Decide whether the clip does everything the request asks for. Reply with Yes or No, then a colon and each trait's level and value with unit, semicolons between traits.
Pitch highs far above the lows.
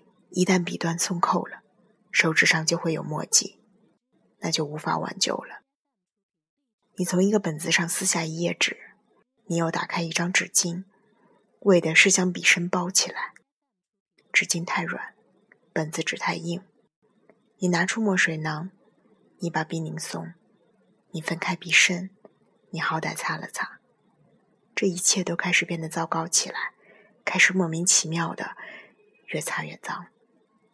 No: average, 3.6 semitones